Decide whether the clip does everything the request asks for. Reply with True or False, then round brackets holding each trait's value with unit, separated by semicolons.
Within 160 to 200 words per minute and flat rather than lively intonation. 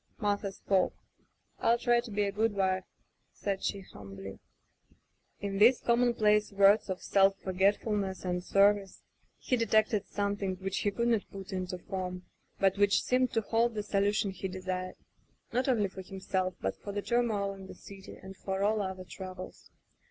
True (175 wpm; 1.9 semitones)